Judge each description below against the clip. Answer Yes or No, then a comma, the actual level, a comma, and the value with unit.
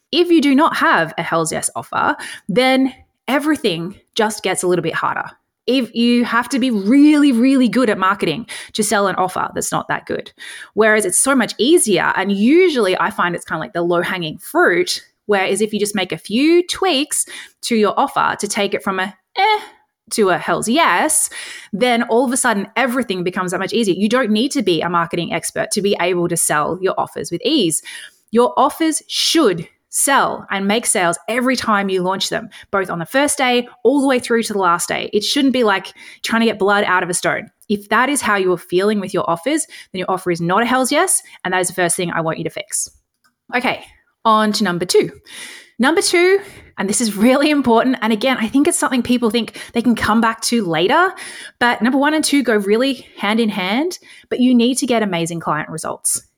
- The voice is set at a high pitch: Yes, high, 225 Hz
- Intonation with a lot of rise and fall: Yes, wide, 6.4 semitones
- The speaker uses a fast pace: Yes, fast, 225 wpm